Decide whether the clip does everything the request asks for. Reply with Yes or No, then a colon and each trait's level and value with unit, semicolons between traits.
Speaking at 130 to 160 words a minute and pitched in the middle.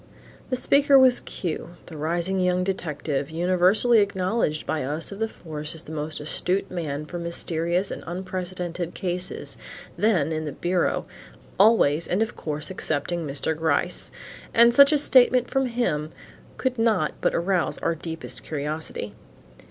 Yes: average, 150 wpm; medium, 175 Hz